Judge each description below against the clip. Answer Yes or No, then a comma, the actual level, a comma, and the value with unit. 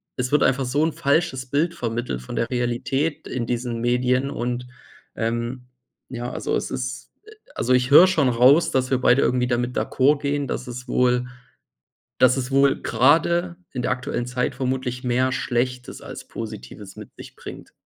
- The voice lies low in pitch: Yes, low, 125 Hz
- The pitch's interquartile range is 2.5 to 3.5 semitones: No, narrow, 2.0 semitones